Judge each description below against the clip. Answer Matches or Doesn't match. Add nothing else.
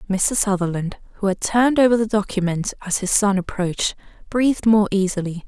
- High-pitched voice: Matches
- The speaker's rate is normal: Matches